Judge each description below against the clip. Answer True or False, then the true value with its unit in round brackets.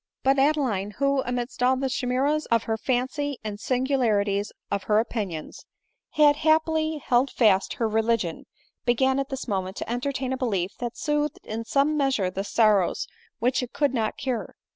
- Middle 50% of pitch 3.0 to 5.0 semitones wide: True (4.3 semitones)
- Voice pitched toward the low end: False (250 Hz)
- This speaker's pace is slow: False (165 wpm)